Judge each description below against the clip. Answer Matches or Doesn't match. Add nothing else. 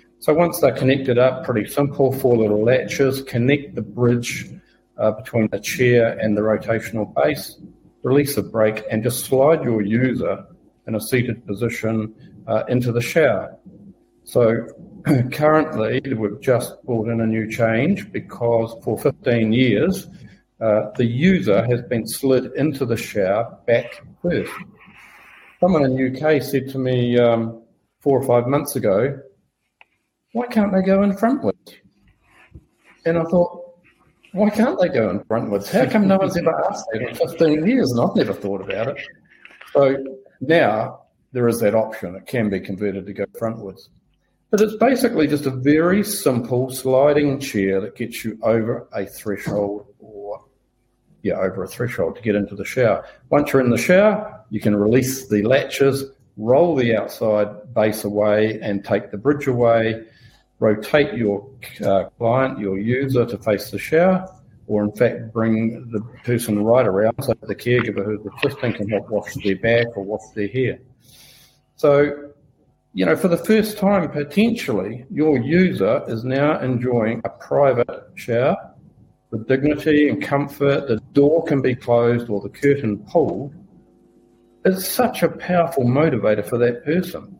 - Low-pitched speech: Matches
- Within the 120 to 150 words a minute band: Doesn't match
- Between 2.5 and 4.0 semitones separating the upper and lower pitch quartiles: Doesn't match